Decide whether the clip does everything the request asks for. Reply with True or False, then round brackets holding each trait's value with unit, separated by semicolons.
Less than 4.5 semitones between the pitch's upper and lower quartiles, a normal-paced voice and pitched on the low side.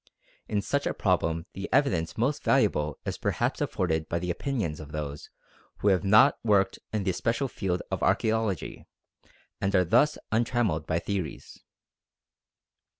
False (5.3 semitones; 150 wpm; 95 Hz)